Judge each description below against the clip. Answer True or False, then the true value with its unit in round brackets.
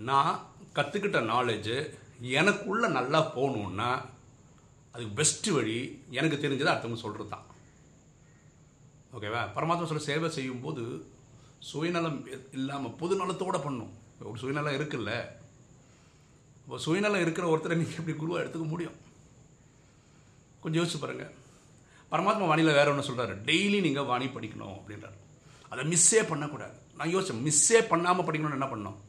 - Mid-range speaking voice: True (145 Hz)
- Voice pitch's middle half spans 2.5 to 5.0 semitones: True (4.3 semitones)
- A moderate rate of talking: True (120 wpm)